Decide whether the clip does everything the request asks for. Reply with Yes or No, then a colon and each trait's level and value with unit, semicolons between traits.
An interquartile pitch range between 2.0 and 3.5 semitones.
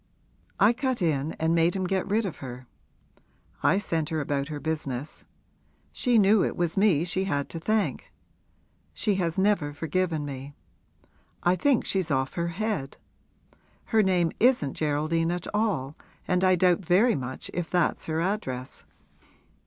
No: average, 4.7 semitones